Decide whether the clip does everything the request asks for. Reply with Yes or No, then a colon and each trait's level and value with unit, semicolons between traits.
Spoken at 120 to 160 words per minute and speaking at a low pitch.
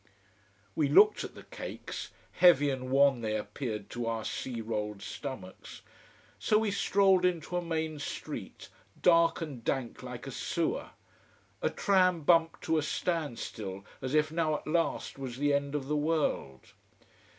No: average, 155 wpm; medium, 145 Hz